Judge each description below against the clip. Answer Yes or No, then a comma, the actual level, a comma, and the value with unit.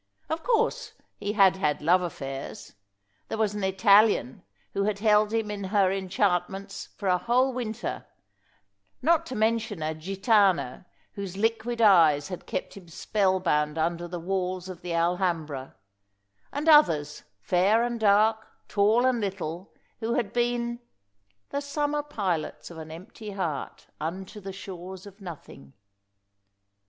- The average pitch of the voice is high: Yes, high, 195 Hz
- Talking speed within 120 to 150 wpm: Yes, average, 145 wpm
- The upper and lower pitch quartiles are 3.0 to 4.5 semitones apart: Yes, average, 4.2 semitones